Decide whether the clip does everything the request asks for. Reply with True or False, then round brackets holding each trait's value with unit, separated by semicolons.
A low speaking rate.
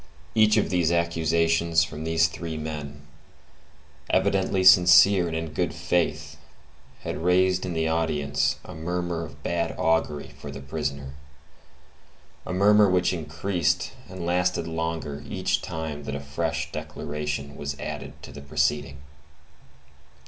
True (130 wpm)